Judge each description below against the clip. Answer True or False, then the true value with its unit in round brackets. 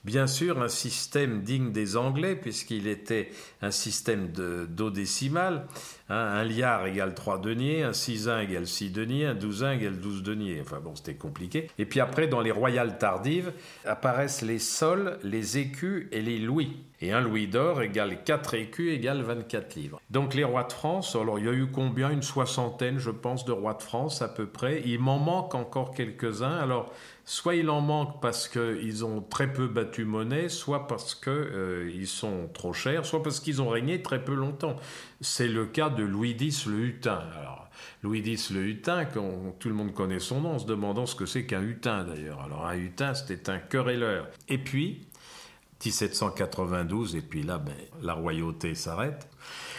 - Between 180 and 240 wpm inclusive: True (190 wpm)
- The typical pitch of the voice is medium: False (120 Hz)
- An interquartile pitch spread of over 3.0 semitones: True (4.8 semitones)